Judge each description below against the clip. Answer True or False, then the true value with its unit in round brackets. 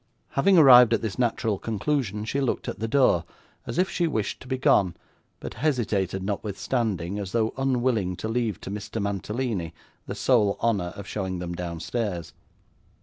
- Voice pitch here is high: False (110 Hz)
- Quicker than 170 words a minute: False (165 wpm)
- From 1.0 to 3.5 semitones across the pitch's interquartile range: False (4.5 semitones)